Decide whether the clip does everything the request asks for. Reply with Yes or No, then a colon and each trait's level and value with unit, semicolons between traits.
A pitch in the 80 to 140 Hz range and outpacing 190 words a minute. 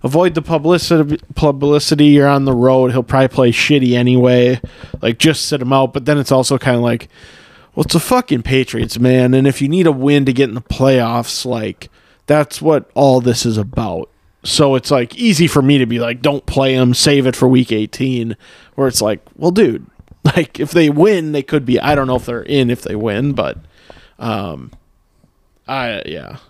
Yes: low, 135 Hz; fast, 205 wpm